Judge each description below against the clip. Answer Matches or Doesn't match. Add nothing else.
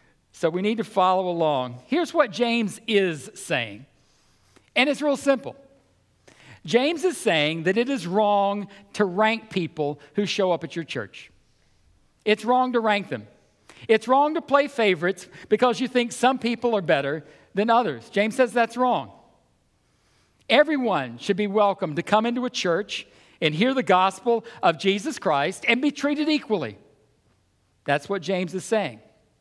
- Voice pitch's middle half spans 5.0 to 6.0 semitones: Matches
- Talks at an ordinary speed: Matches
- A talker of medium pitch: Doesn't match